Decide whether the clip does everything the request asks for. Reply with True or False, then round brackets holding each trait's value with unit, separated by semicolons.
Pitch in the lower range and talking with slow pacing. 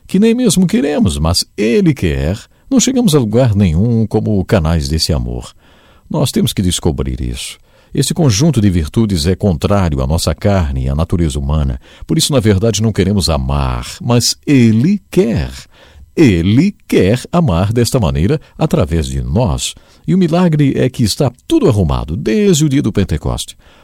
False (105 Hz; 165 wpm)